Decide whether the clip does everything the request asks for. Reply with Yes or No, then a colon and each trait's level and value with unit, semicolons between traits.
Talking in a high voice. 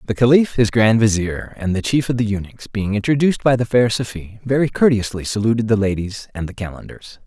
No: low, 110 Hz